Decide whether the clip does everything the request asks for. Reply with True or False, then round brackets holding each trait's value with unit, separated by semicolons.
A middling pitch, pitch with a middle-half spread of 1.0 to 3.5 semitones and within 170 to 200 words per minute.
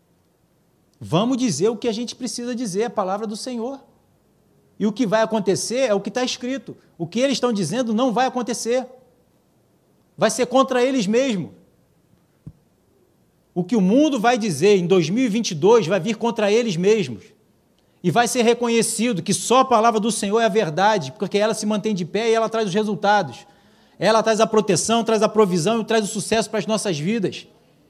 False (220 Hz; 2.8 semitones; 185 wpm)